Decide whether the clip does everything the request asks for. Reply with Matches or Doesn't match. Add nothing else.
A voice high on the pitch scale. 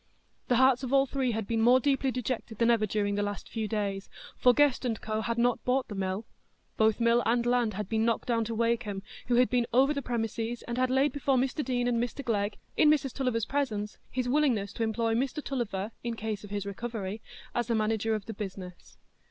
Matches